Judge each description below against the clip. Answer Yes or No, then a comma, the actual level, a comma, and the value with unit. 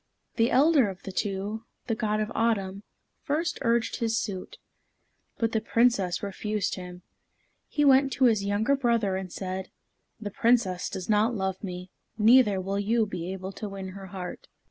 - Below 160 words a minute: No, average, 165 wpm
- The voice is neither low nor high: No, high, 210 Hz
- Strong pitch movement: No, average, 3.4 semitones